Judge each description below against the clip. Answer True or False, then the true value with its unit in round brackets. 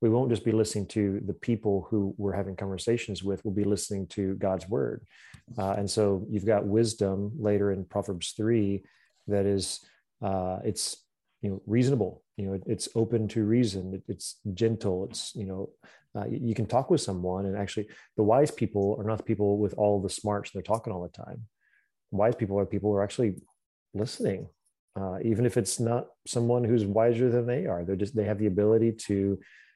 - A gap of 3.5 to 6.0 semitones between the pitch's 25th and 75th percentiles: False (2.5 semitones)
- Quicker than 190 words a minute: True (200 wpm)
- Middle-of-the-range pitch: False (105 Hz)